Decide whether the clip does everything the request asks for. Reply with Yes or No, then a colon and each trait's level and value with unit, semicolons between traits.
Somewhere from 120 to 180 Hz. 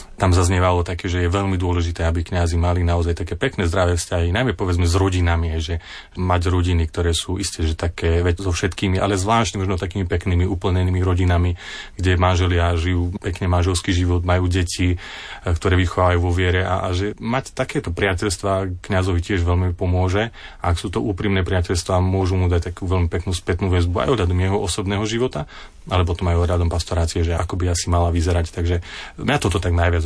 No: very low, 90 Hz